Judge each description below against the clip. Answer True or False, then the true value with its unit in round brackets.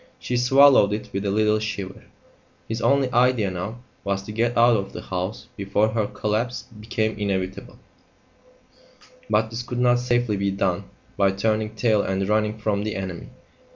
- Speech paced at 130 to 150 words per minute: False (165 wpm)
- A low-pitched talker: True (110 Hz)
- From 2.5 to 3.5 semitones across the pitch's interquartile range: True (2.9 semitones)